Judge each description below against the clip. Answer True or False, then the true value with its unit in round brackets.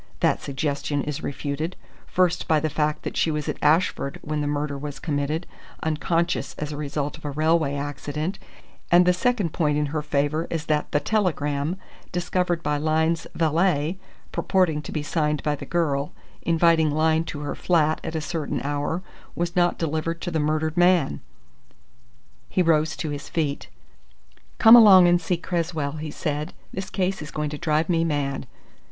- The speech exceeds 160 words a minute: True (175 wpm)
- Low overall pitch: False (155 Hz)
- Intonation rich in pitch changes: False (2.6 semitones)